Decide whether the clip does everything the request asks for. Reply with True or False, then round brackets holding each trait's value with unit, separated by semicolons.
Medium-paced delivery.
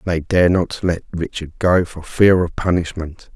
True (195 wpm)